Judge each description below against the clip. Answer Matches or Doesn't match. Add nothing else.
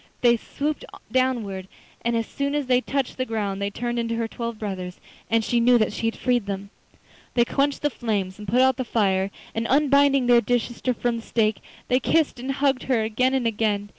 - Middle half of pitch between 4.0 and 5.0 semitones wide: Doesn't match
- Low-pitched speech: Doesn't match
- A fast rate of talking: Matches